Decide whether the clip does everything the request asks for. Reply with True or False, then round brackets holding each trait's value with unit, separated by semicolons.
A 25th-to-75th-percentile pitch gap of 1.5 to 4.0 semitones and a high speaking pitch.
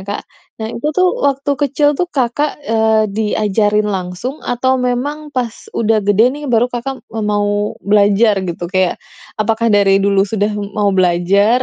True (3.6 semitones; 220 Hz)